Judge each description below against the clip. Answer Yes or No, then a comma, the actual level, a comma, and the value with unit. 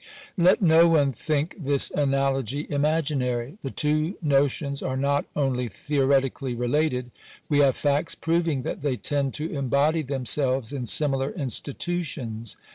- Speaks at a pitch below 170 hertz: Yes, medium, 140 Hz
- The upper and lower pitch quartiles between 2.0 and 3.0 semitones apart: Yes, narrow, 2.4 semitones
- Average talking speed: No, slow, 130 wpm